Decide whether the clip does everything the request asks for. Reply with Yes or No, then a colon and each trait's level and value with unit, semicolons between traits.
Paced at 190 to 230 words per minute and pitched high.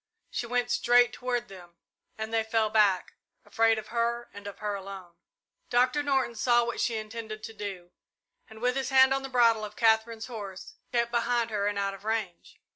Yes: average, 195 wpm; high, 225 Hz